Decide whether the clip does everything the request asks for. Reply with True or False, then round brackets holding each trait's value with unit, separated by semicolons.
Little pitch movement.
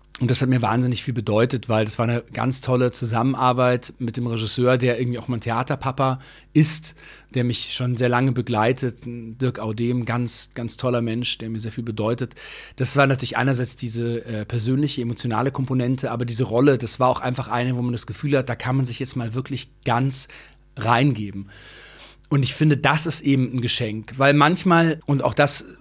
True (2.0 semitones)